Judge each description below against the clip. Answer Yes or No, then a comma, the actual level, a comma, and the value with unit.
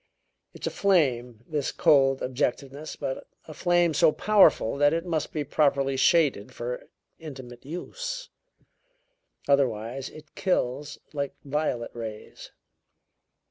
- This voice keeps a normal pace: No, slow, 115 wpm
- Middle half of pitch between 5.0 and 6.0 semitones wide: No, average, 3.8 semitones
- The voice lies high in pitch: No, medium, 140 Hz